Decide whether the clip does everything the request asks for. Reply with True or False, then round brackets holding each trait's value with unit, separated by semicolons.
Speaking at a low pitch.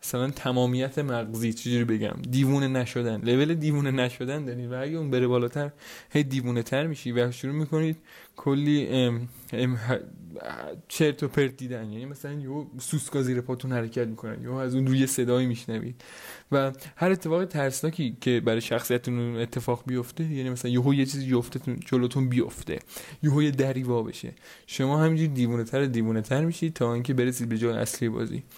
True (130 Hz)